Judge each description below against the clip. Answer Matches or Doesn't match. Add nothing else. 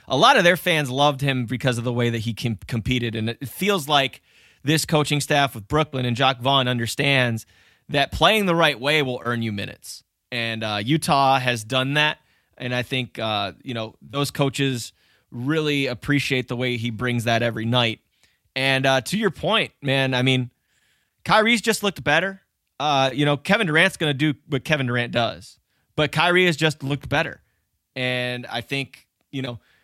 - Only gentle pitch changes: Doesn't match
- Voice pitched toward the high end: Doesn't match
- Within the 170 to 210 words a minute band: Matches